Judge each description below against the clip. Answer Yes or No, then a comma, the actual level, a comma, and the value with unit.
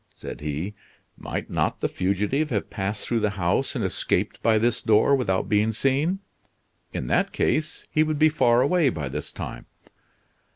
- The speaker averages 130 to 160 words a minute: No, average, 170 wpm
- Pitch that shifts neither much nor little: No, wide, 6.1 semitones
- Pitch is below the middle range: Yes, low, 110 Hz